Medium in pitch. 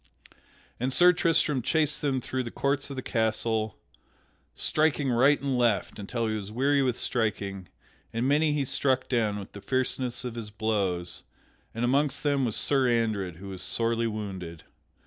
No: low, 120 Hz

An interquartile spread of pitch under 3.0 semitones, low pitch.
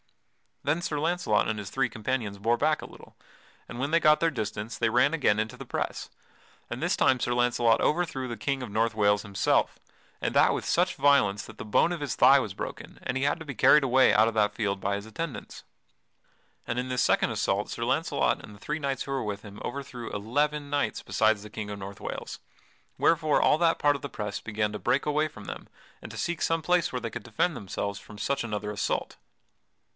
No: wide, 5.5 semitones; low, 120 Hz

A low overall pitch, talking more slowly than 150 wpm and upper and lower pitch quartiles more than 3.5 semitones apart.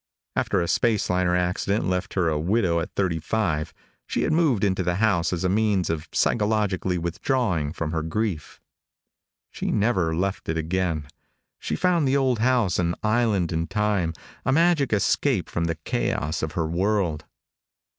No: very low, 95 Hz; average, 165 wpm; average, 4.7 semitones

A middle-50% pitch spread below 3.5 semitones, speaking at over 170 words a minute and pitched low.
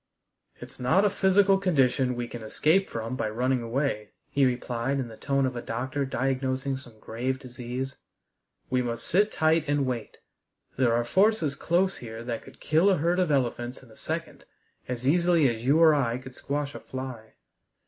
No: average, 4.2 semitones; average, 185 wpm; low, 130 Hz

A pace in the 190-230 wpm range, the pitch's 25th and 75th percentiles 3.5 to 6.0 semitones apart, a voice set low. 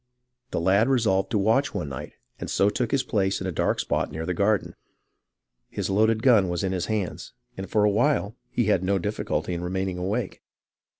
No: average, 200 wpm; average, 2.9 semitones; low, 100 Hz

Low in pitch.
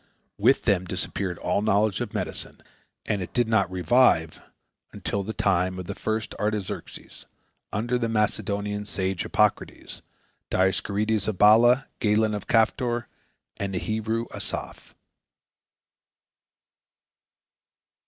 Yes: low, 105 Hz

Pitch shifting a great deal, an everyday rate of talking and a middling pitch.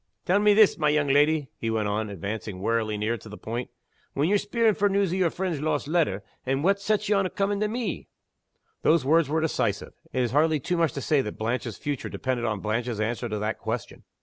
No: wide, 8.1 semitones; fast, 225 wpm; medium, 145 Hz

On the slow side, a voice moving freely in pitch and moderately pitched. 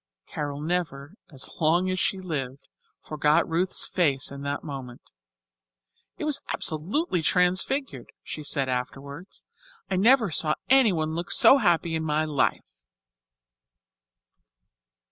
No: slow, 120 wpm; average, 4.4 semitones; medium, 160 Hz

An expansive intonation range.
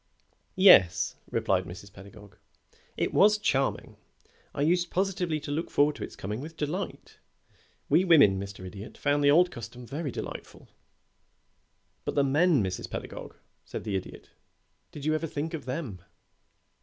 Yes: wide, 8.1 semitones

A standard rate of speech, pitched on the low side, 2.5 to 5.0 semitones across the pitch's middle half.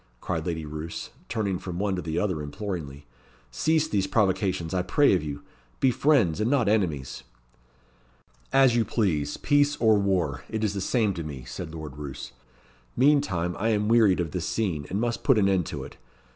No: average, 185 wpm; very low, 95 Hz; wide, 5.6 semitones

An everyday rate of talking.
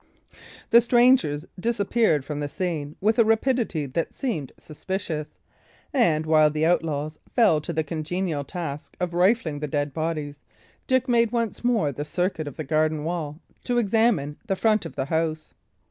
Yes: average, 160 wpm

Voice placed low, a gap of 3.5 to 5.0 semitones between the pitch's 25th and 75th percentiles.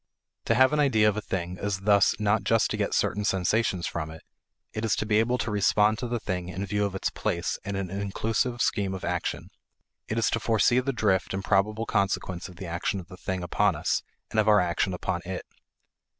No: low, 100 Hz; average, 2.7 semitones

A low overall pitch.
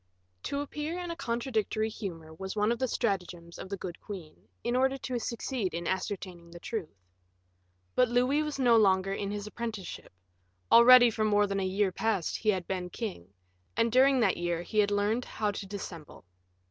No: high, 210 Hz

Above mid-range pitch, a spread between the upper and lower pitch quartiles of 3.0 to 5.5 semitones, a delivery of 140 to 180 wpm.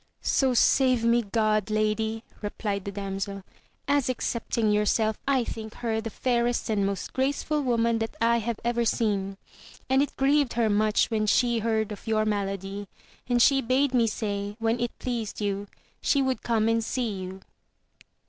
No: high, 225 Hz; narrow, 2.6 semitones; average, 165 wpm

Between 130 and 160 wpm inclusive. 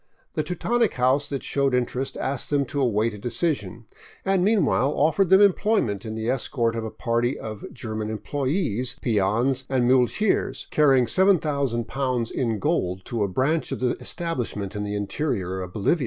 No: average, 170 wpm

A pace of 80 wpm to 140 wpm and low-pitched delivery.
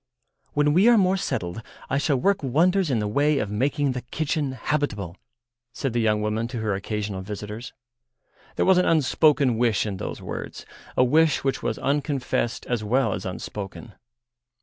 No: average, 170 wpm; low, 125 Hz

